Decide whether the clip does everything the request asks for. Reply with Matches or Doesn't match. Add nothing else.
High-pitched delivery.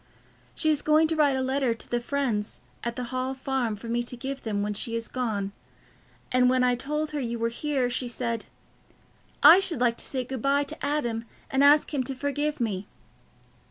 Matches